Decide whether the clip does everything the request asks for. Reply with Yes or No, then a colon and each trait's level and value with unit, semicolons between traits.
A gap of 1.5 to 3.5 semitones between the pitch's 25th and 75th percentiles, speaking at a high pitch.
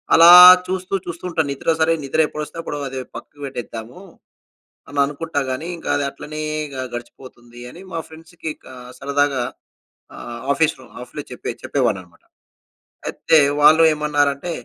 No: average, 3.2 semitones; medium, 145 Hz